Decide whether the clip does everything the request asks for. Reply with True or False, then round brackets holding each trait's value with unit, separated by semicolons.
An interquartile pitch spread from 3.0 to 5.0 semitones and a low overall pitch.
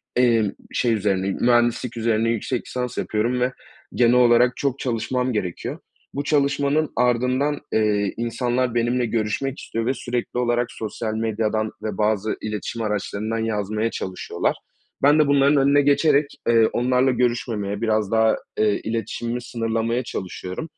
False (2.5 semitones; 115 Hz)